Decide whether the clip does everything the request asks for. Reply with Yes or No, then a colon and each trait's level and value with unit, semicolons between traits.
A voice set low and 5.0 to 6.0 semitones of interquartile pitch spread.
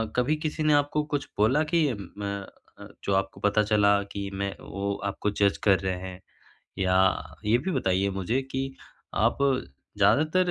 Yes: low, 100 Hz; wide, 5.5 semitones